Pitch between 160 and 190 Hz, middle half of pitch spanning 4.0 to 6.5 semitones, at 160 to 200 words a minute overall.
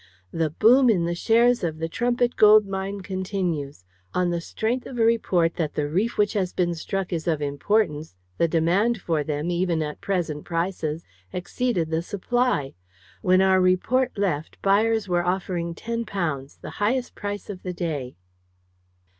Yes: medium, 185 Hz; average, 4.4 semitones; average, 165 wpm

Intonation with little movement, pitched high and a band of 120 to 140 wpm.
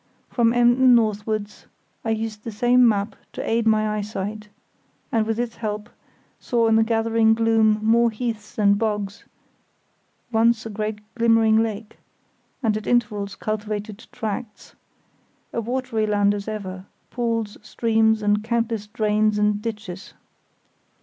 Yes: narrow, 1.5 semitones; high, 220 Hz; slow, 135 wpm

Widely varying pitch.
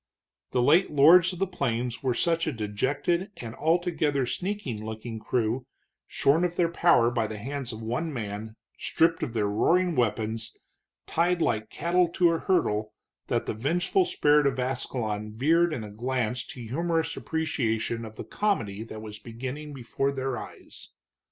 Yes: wide, 6.7 semitones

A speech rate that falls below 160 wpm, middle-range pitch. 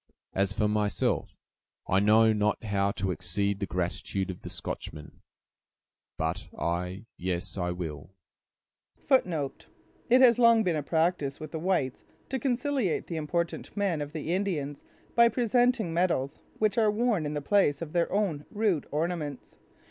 Yes: average, 150 wpm; medium, 150 Hz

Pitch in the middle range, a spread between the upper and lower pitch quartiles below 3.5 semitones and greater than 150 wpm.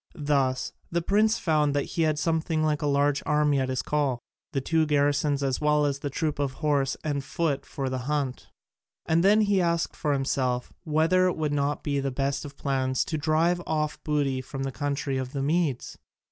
Yes: medium, 145 Hz; narrow, 2.4 semitones; average, 200 wpm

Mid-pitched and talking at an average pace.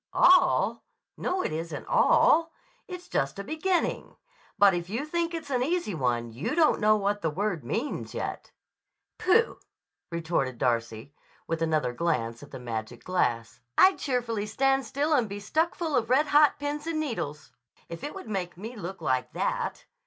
No: high, 205 Hz; average, 170 wpm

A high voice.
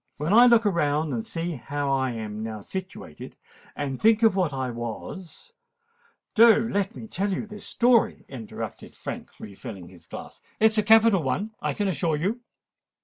No: medium, 170 Hz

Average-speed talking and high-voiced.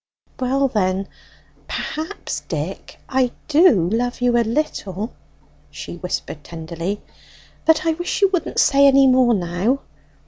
No: slow, 130 wpm; high, 245 Hz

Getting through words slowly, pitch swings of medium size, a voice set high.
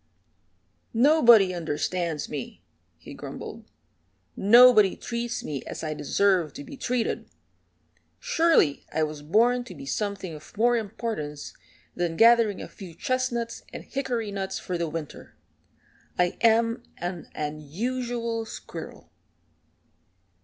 No: slow, 115 wpm; wide, 6.4 semitones; high, 205 Hz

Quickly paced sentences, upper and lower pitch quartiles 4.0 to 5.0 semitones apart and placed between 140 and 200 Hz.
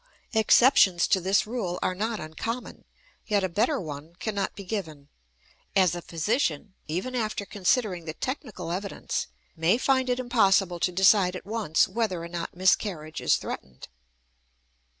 No: average, 150 wpm; average, 4.4 semitones; high, 190 Hz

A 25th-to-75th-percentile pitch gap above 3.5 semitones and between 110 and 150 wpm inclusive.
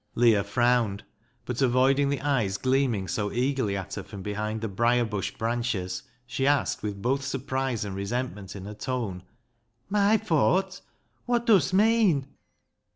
No: average, 4.9 semitones; average, 160 wpm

